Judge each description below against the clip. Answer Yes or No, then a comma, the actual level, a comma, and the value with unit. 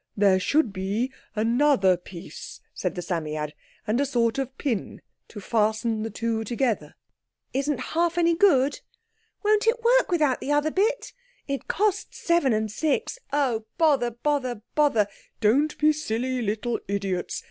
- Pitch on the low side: No, very high, 255 Hz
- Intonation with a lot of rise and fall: Yes, wide, 6.4 semitones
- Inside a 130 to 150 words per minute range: Yes, slow, 135 wpm